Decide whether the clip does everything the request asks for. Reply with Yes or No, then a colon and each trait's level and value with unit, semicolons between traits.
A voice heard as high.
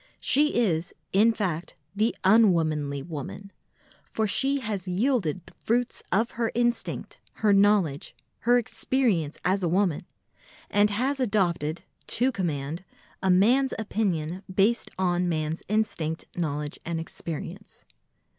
Yes: high, 195 Hz